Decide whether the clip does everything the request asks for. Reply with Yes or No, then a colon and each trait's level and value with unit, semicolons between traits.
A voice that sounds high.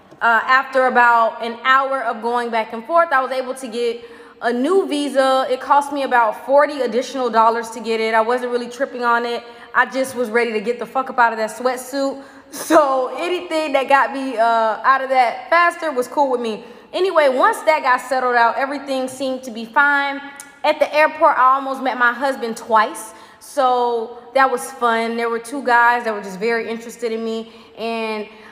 Yes: very high, 250 Hz